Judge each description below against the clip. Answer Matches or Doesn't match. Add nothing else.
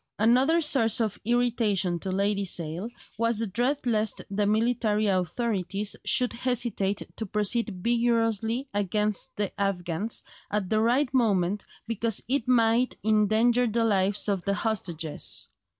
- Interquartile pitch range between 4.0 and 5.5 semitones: Doesn't match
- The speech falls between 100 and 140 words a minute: Matches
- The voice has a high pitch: Matches